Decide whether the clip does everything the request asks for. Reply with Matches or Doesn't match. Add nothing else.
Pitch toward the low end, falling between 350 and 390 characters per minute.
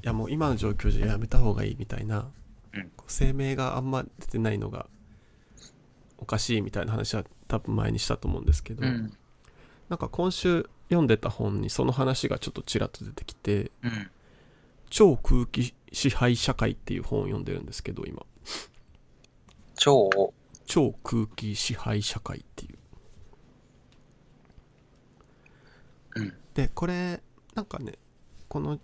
Doesn't match